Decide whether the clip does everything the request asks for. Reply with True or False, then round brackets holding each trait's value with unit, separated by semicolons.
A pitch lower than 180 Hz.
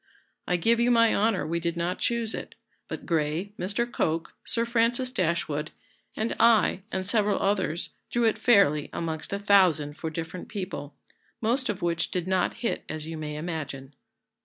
False (185 Hz)